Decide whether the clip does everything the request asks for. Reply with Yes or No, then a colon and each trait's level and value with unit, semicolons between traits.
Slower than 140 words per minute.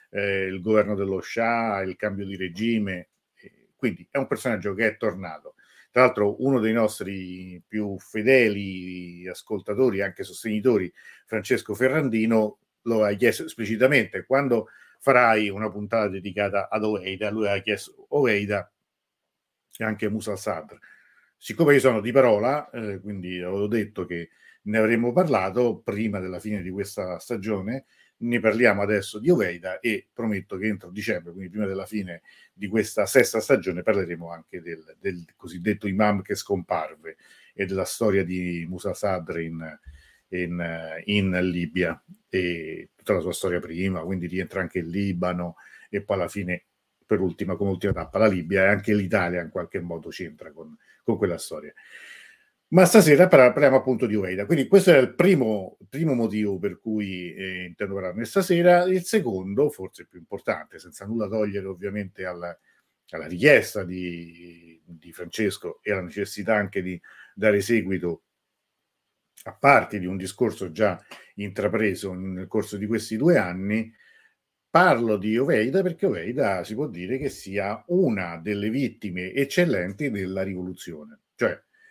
No: average, 150 wpm